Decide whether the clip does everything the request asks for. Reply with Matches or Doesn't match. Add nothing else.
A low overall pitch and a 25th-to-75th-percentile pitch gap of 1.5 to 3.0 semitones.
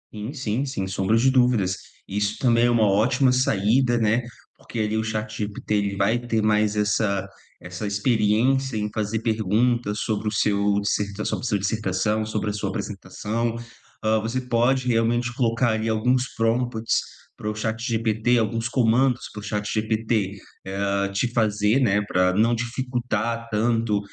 Matches